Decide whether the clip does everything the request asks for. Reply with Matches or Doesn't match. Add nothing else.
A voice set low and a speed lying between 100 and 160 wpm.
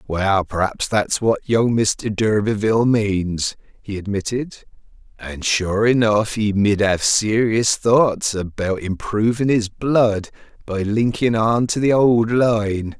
Matches